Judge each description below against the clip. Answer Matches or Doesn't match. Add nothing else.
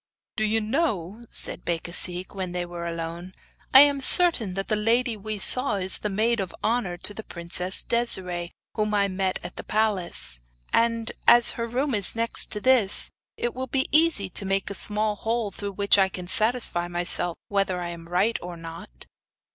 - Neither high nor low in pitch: Doesn't match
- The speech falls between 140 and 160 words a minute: Doesn't match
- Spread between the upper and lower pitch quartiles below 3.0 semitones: Doesn't match